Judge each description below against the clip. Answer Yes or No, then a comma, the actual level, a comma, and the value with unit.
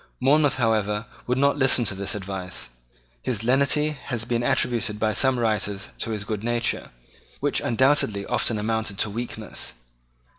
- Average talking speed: Yes, average, 150 wpm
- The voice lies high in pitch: No, low, 115 Hz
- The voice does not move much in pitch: No, average, 3.5 semitones